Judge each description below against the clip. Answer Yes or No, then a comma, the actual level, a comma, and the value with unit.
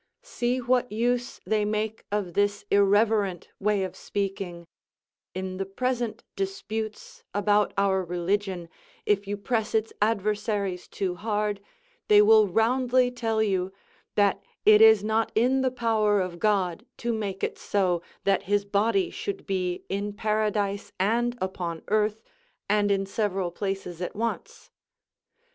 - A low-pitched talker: No, high, 205 Hz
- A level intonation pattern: Yes, narrow, 2.3 semitones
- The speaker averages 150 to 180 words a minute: No, average, 140 wpm